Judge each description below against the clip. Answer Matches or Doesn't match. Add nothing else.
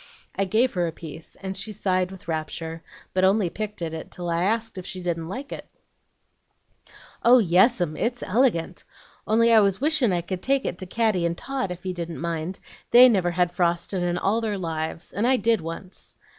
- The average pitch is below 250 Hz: Matches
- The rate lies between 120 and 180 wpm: Doesn't match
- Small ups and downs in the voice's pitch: Doesn't match